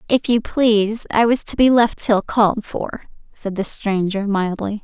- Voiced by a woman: Yes, female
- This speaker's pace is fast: No, average, 185 wpm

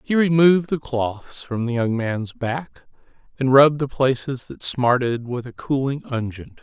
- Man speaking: Yes, male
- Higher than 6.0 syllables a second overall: No, 4.4 syllables/s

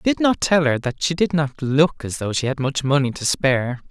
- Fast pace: Yes, fast, 290 wpm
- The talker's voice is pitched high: No, medium, 145 Hz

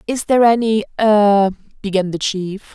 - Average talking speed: No, slow, 130 wpm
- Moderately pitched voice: No, high, 210 Hz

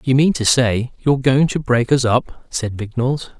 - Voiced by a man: Yes, male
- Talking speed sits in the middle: No, fast, 210 wpm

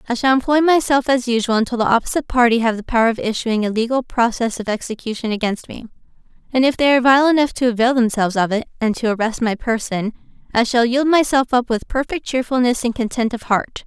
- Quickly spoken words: Yes, fast, 215 wpm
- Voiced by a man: No, female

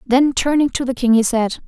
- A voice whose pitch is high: Yes, very high, 255 Hz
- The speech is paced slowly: No, fast, 250 wpm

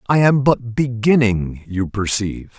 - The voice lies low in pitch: Yes, low, 115 Hz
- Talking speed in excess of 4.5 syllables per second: No, 4.4 syllables/s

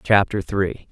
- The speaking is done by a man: Yes, male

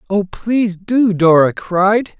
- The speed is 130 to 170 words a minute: Yes, slow, 135 wpm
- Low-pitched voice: No, high, 200 Hz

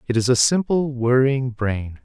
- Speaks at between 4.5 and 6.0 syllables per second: No, 4.3 syllables/s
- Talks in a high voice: No, low, 125 Hz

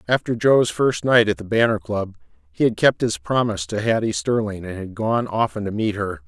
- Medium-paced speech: No, fast, 220 wpm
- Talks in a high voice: No, low, 110 Hz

